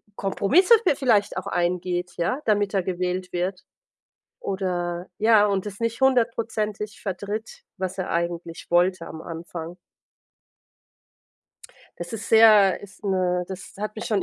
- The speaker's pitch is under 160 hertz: No, high, 190 Hz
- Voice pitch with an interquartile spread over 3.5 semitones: No, average, 3.1 semitones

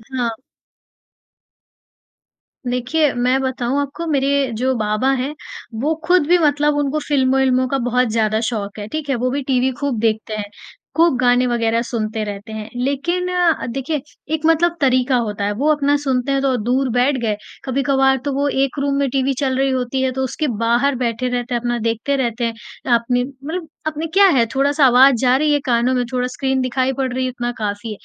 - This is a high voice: Yes, very high, 260 Hz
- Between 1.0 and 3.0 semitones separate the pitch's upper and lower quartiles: Yes, average, 2.7 semitones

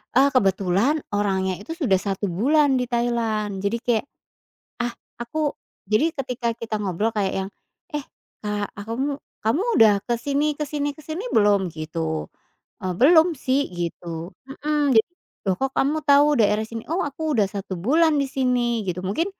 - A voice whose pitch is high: Yes, high, 235 Hz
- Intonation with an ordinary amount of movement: No, wide, 6.1 semitones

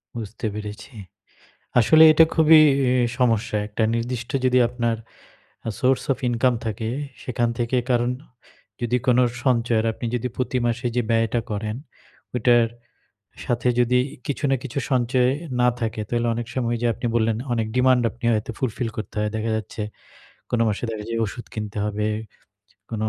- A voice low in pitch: Yes, low, 120 Hz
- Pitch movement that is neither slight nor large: No, narrow, 2.1 semitones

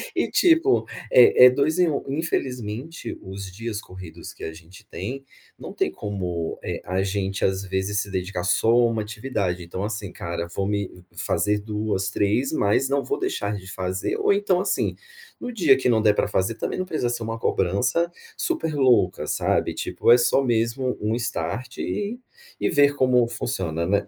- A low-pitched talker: Yes, low, 110 Hz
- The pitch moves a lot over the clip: Yes, wide, 5.8 semitones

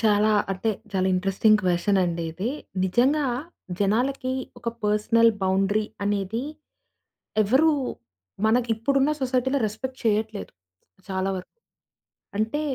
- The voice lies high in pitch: Yes, high, 215 Hz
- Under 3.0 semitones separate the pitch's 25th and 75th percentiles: No, average, 4.1 semitones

